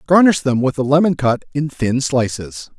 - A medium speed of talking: Yes, average, 195 wpm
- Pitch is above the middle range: No, medium, 140 Hz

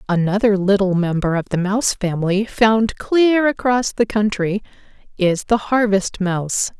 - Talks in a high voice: Yes, high, 205 Hz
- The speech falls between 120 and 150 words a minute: Yes, average, 140 wpm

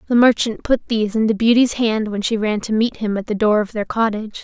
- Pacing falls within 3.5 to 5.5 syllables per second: No, 5.9 syllables/s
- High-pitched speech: Yes, high, 220 Hz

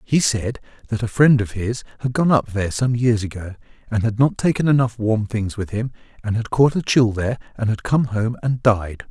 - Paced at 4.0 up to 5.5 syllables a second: Yes, 5.3 syllables/s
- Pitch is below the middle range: Yes, low, 115 Hz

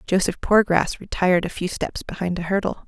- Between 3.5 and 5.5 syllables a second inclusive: No, 5.7 syllables/s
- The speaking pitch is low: No, medium, 185 Hz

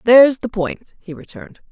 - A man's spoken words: No, female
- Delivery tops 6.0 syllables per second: No, 5.3 syllables/s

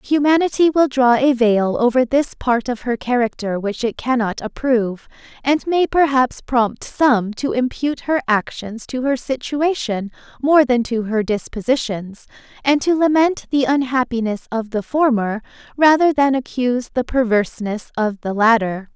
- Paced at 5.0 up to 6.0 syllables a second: No, 4.6 syllables/s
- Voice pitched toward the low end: No, very high, 250 Hz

